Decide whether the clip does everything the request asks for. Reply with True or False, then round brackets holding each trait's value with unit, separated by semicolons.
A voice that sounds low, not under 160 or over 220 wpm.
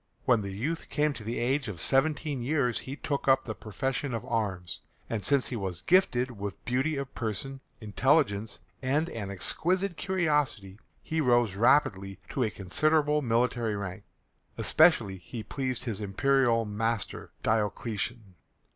False (120 Hz; 145 wpm)